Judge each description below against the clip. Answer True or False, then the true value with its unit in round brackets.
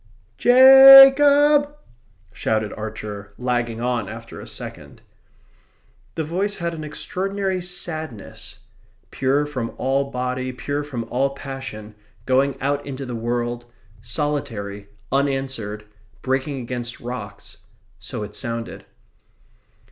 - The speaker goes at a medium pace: False (110 wpm)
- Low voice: True (130 Hz)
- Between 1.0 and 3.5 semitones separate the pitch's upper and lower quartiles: False (4.7 semitones)